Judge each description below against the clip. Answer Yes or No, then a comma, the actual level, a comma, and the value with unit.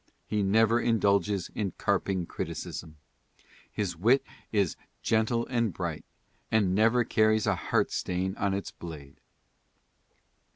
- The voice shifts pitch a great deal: No, average, 3.3 semitones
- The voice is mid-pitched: No, low, 100 Hz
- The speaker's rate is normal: No, slow, 115 wpm